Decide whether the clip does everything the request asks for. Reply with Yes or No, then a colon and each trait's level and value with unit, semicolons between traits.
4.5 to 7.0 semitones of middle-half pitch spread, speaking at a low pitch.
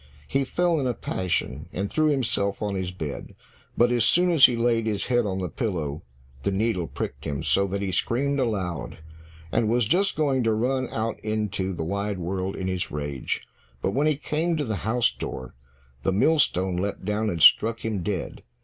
Yes: average, 4.9 semitones; low, 105 Hz